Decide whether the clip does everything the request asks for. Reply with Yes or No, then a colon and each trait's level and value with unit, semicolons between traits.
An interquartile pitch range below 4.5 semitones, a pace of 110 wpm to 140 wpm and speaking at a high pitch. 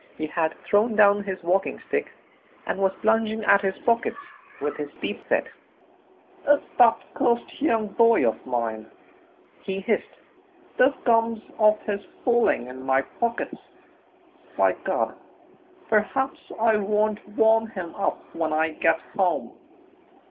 Yes: average, 3.5 semitones; slow, 135 wpm; high, 210 Hz